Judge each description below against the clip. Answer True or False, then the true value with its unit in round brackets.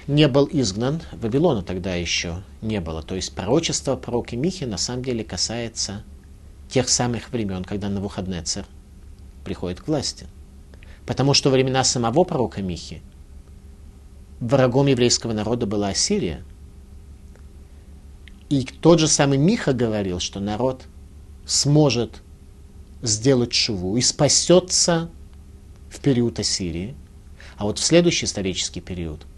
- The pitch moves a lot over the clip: True (7.7 semitones)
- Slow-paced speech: False (125 wpm)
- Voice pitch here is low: True (95 Hz)